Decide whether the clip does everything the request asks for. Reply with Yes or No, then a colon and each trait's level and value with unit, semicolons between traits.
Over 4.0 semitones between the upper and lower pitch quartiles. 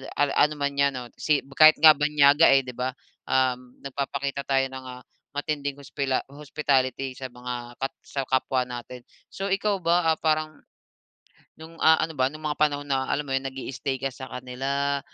No: narrow, 2.4 semitones